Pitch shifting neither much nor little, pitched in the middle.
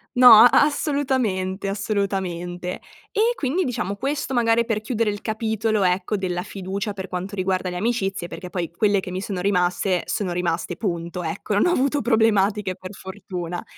No: average, 3.7 semitones; high, 200 Hz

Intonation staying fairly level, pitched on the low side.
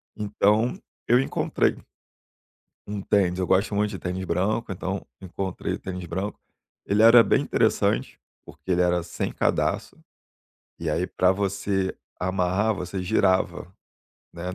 Yes: narrow, 2.2 semitones; very low, 95 Hz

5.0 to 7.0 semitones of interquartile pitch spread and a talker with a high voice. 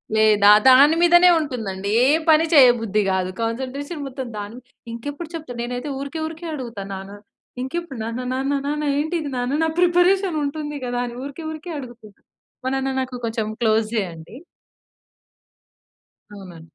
Yes: wide, 5.4 semitones; very high, 260 Hz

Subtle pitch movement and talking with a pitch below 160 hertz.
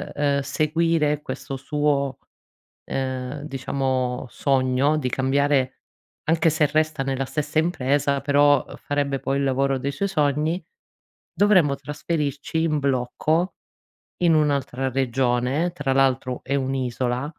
Yes: narrow, 2.3 semitones; medium, 140 Hz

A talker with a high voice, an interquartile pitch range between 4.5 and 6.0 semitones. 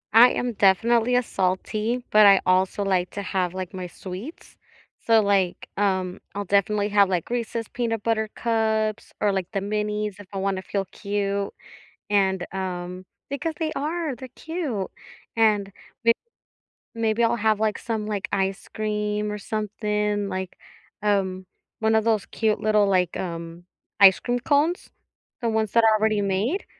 No: high, 210 Hz; average, 2.7 semitones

